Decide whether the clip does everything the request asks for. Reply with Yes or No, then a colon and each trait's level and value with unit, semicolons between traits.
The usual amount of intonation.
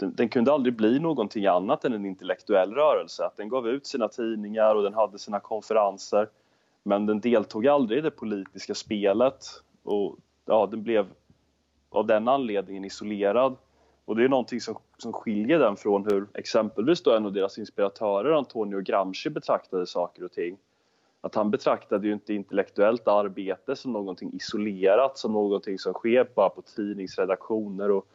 No: narrow, 1.9 semitones